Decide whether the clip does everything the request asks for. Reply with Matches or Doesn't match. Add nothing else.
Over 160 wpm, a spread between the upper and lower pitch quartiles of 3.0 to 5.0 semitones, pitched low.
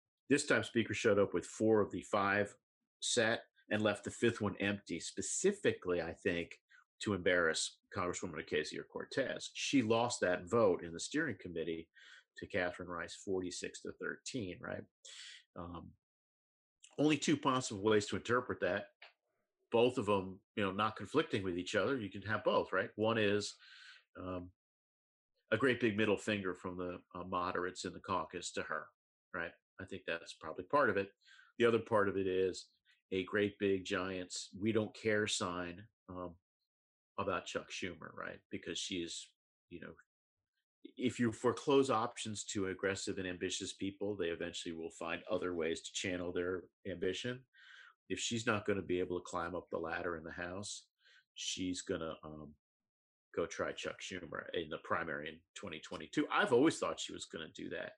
Matches